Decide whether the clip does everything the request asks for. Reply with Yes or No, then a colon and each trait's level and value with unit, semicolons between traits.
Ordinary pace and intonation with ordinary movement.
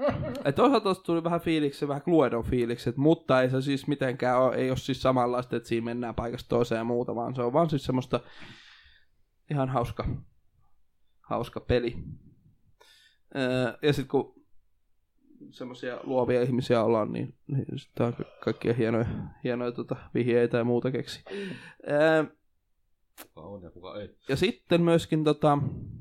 Yes: average, 135 wpm; average, 3.7 semitones